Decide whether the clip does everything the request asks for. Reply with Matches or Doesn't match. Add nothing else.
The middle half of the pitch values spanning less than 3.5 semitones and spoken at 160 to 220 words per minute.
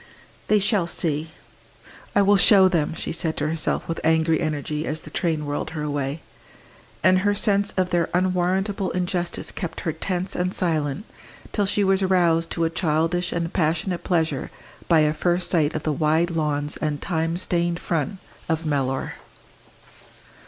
Matches